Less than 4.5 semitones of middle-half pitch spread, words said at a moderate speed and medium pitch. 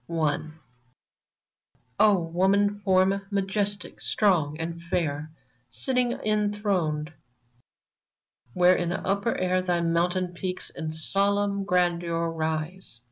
No: average, 3.2 semitones; slow, 90 wpm; medium, 180 Hz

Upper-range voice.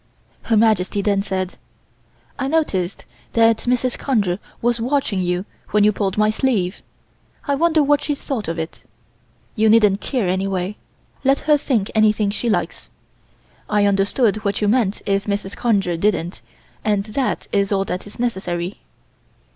Yes: high, 210 Hz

